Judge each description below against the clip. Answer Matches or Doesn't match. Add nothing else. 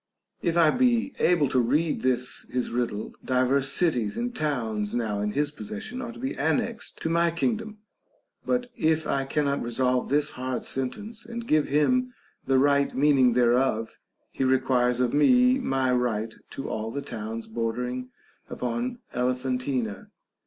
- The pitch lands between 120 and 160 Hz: Matches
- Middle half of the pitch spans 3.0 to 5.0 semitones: Doesn't match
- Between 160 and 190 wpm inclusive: Doesn't match